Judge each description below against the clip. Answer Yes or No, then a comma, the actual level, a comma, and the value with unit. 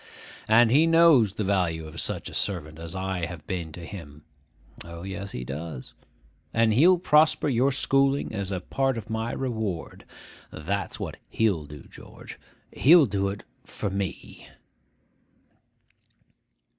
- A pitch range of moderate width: No, wide, 6.2 semitones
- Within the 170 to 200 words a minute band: No, average, 145 wpm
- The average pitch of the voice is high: No, low, 100 Hz